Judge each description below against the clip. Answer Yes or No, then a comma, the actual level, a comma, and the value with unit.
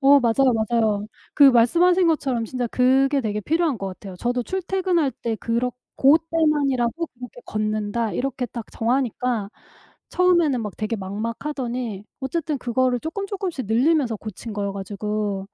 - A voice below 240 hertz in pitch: No, high, 245 Hz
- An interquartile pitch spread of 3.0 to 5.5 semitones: Yes, average, 5.1 semitones